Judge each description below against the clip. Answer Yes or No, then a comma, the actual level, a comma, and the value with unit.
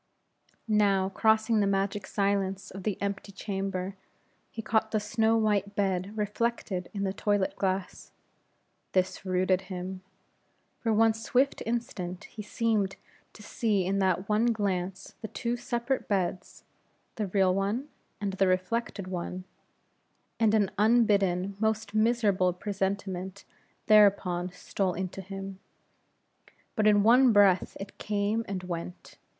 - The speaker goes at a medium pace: No, slow, 130 wpm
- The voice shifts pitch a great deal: No, narrow, 2.4 semitones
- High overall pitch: Yes, high, 200 Hz